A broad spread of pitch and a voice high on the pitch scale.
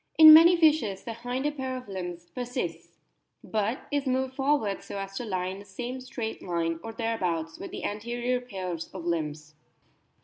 Yes: wide, 5.8 semitones; high, 225 Hz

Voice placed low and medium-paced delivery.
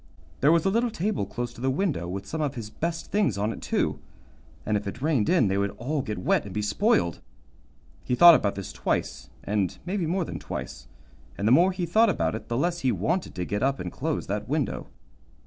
No: low, 130 Hz; fast, 230 wpm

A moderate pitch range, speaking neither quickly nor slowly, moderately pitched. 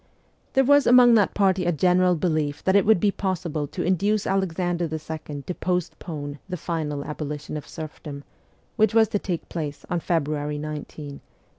Yes: average, 4.1 semitones; average, 170 wpm; medium, 170 Hz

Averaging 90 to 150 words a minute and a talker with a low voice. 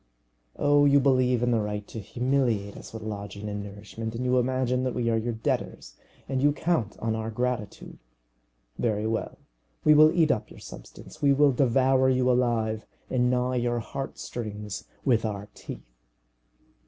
No: average, 170 wpm; low, 120 Hz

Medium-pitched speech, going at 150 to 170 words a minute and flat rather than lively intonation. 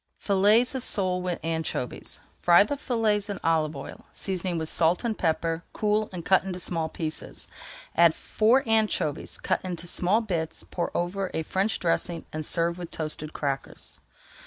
No: medium, 175 Hz; average, 160 wpm; average, 4.0 semitones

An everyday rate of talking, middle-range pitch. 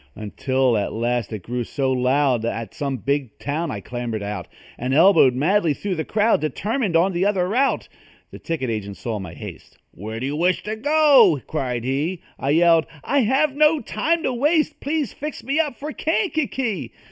Yes: average, 185 wpm; medium, 160 Hz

